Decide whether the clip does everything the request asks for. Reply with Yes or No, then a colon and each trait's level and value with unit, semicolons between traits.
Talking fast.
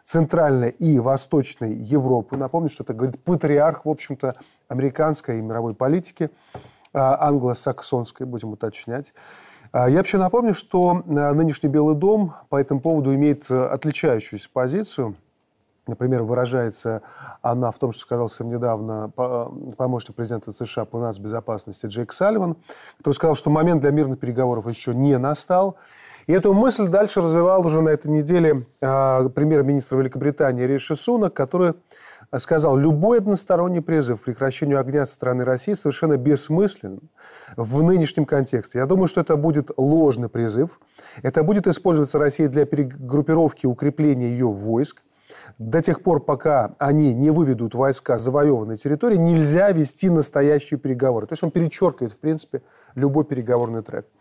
No: average, 140 wpm